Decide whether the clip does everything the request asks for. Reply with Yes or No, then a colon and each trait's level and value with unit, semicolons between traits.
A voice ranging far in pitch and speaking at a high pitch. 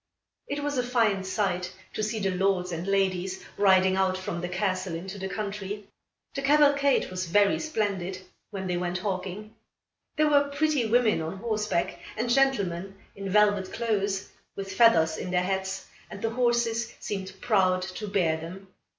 No: average, 3.2 semitones; high, 195 Hz